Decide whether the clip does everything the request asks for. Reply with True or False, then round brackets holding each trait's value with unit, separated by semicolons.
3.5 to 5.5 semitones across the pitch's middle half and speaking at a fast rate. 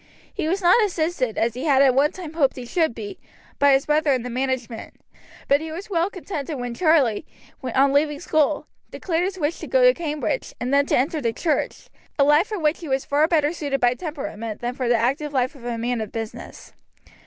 True (4.3 semitones; 220 wpm)